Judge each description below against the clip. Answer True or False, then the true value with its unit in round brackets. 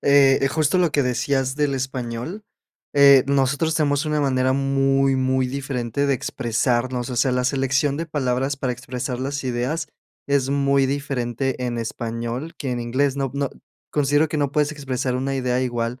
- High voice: False (135 Hz)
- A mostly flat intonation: True (2.0 semitones)